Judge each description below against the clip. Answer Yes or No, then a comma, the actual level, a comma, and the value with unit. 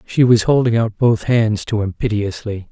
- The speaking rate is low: No, average, 200 wpm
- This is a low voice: Yes, low, 110 Hz